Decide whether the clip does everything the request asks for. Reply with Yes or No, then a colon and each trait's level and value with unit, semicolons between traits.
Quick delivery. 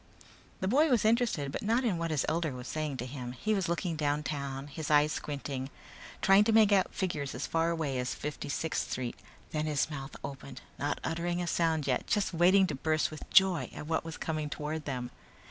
Yes: fast, 210 wpm